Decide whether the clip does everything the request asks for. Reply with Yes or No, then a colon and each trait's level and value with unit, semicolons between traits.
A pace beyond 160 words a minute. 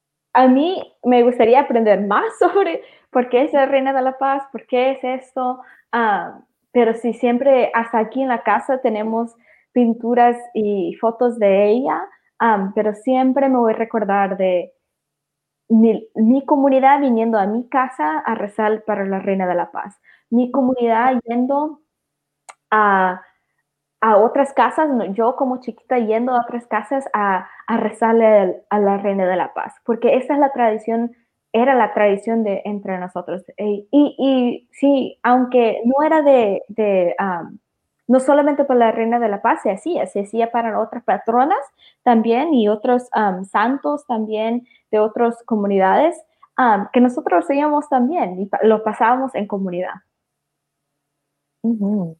No: average, 155 wpm